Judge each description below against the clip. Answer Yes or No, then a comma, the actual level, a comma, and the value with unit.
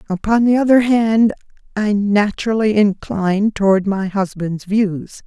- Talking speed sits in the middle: No, slow, 125 wpm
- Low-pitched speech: No, high, 205 Hz